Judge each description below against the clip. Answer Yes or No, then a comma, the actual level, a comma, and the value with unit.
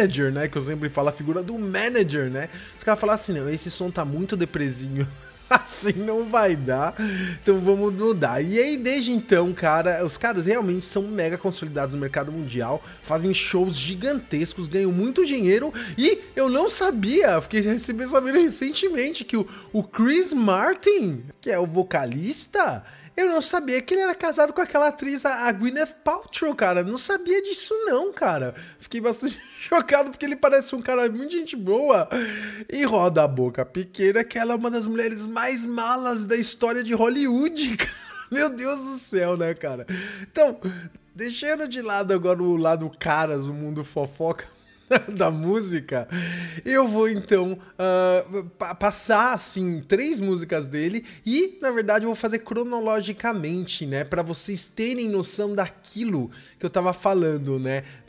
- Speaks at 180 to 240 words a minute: No, average, 165 wpm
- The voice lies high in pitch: Yes, high, 205 Hz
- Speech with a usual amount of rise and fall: No, wide, 6.4 semitones